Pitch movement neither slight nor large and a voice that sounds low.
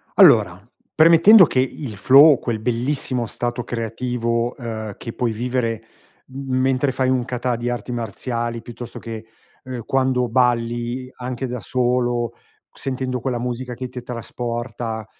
No: narrow, 1.7 semitones; low, 120 Hz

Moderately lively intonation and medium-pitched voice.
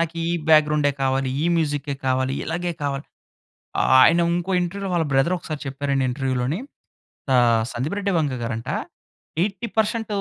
Yes: average, 4.7 semitones; medium, 150 Hz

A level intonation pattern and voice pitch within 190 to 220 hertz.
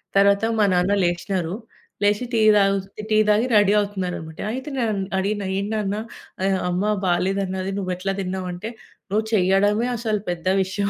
Yes: narrow, 2.0 semitones; high, 195 Hz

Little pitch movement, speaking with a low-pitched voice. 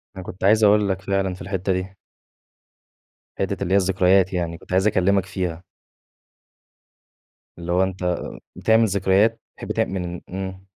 Yes: narrow, 1.3 semitones; very low, 95 Hz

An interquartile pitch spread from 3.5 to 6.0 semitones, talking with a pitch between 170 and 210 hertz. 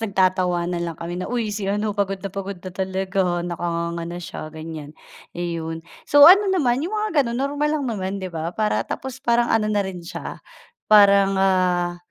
Yes: average, 4.3 semitones; high, 190 Hz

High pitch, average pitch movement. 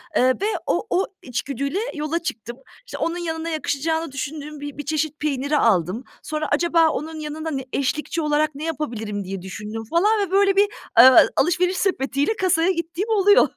Yes: very high, 305 Hz; average, 3.6 semitones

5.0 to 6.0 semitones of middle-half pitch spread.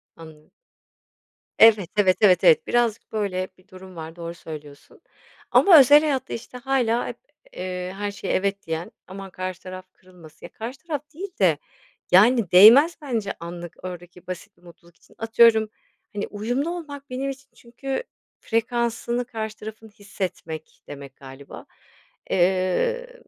Yes: average, 5.3 semitones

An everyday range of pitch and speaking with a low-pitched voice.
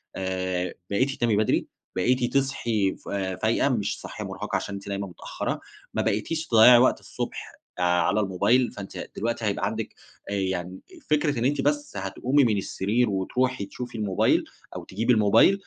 Yes: average, 4.4 semitones; low, 105 Hz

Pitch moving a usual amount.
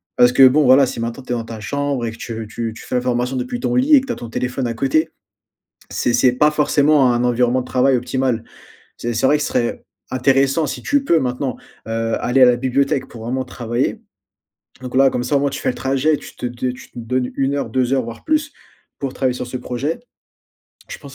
No: narrow, 2.3 semitones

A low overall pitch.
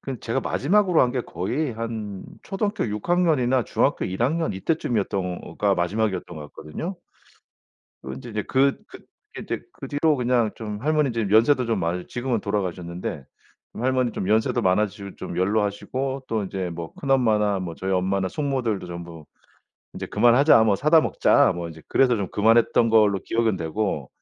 Yes: low, 110 Hz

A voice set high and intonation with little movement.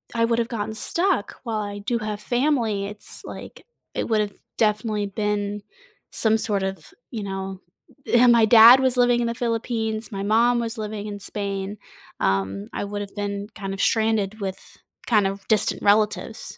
Yes: high, 210 Hz; narrow, 2.3 semitones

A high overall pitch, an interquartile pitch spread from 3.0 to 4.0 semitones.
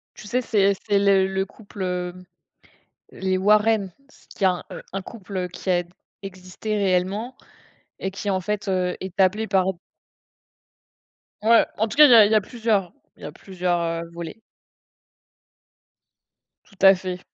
No: high, 195 Hz; narrow, 2.5 semitones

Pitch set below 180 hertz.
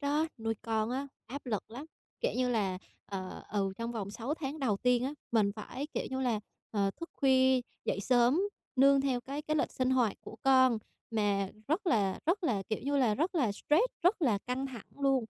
No: very high, 255 Hz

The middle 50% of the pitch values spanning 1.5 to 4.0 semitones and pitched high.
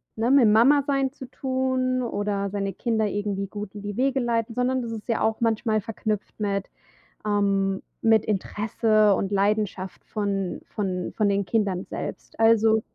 Yes: narrow, 2.6 semitones; high, 215 Hz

